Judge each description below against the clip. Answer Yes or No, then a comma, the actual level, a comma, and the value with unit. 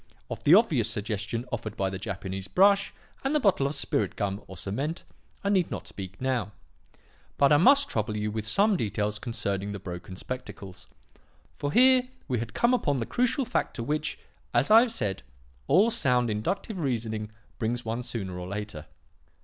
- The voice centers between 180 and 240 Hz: No, low, 120 Hz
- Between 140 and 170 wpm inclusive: No, average, 180 wpm